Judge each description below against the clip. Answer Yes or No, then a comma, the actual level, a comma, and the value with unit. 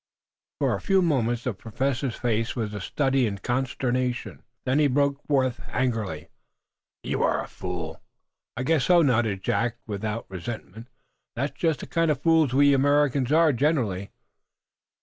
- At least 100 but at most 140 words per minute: No, average, 160 wpm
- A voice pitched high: No, low, 125 Hz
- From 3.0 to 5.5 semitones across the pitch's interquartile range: Yes, average, 4.2 semitones